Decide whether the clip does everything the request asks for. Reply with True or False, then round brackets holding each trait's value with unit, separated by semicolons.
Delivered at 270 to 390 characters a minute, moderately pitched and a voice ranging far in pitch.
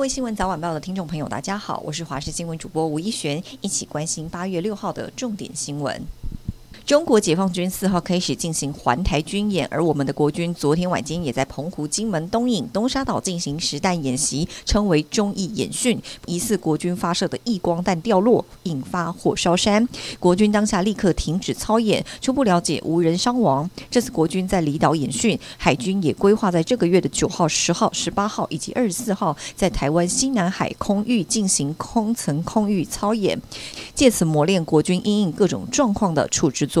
False (305 characters per minute; 180 Hz; 5.0 semitones)